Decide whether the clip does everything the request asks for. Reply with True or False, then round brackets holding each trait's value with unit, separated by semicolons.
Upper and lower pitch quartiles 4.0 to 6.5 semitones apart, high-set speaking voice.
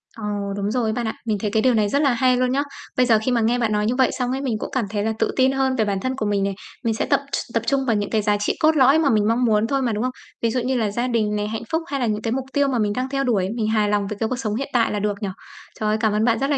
False (3.5 semitones; 230 Hz)